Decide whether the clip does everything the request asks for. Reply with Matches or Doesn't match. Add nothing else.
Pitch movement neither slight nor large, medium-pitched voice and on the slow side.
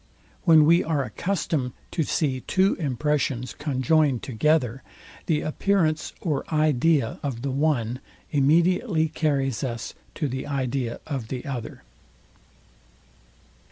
Matches